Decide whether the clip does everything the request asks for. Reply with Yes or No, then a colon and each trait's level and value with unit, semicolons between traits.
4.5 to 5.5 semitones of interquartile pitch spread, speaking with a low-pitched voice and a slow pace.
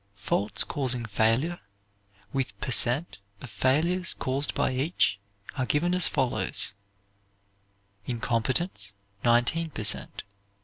Yes: average, 5.2 semitones; low, 130 Hz; slow, 105 wpm